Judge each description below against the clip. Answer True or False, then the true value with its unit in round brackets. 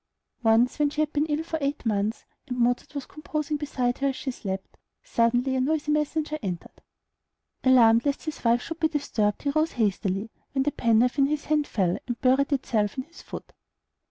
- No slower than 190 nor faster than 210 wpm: True (195 wpm)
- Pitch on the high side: True (265 Hz)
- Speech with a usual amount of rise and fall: True (4.5 semitones)